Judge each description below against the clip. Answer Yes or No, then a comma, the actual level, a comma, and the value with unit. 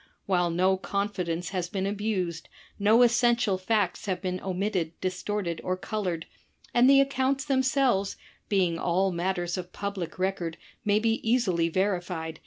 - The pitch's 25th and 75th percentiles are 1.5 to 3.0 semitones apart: No, average, 3.4 semitones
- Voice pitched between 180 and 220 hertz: Yes, high, 190 Hz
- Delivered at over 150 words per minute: No, average, 140 wpm